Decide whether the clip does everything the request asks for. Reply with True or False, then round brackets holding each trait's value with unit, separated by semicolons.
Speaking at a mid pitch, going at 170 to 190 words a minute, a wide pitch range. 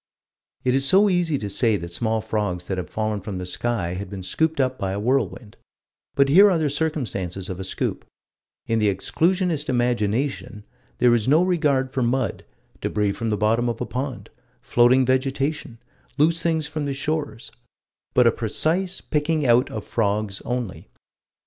False (125 Hz; 175 wpm; 5.8 semitones)